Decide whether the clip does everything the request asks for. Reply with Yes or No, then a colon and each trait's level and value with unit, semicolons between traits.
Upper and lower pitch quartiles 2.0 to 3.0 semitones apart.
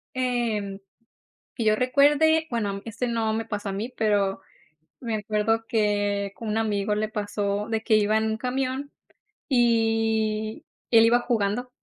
Yes: narrow, 2.4 semitones